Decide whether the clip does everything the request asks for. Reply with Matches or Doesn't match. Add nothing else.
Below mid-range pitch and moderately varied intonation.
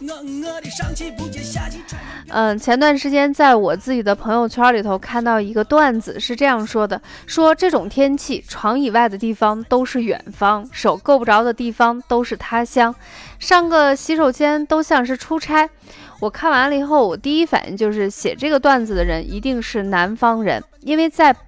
Doesn't match